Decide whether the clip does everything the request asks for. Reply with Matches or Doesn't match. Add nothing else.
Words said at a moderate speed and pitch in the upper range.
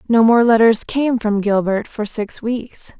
Matches